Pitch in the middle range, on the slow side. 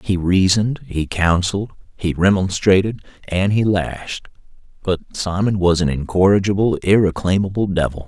No: very low, 95 Hz; slow, 120 wpm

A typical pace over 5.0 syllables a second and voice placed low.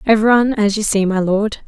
No: 5.8 syllables/s; high, 210 Hz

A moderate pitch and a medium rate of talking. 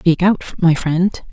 Yes: medium, 175 Hz; average, 180 wpm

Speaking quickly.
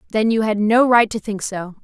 Yes: fast, 260 wpm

